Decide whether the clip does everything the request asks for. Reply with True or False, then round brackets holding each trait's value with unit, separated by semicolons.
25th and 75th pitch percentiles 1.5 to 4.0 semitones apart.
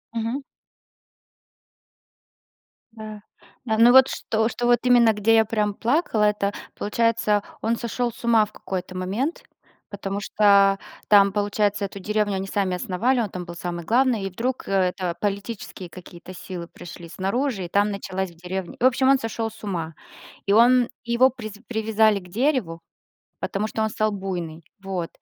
True (3.2 semitones)